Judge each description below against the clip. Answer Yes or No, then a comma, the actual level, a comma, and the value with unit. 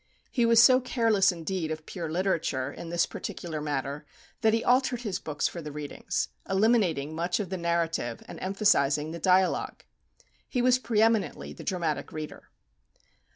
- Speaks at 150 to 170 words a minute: Yes, average, 160 wpm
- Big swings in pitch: Yes, wide, 6.1 semitones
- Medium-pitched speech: Yes, medium, 180 Hz